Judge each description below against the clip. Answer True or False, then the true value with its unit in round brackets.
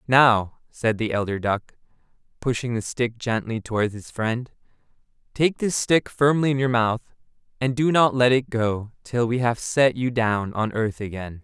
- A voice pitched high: False (120 Hz)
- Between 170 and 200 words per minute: True (180 wpm)